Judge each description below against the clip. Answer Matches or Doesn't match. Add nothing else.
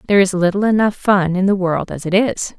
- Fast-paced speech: Matches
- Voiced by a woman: Matches